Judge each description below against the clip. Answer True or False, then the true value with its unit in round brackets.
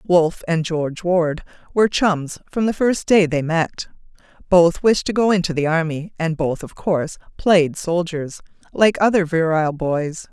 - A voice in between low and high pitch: True (170 Hz)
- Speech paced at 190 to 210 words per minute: False (170 wpm)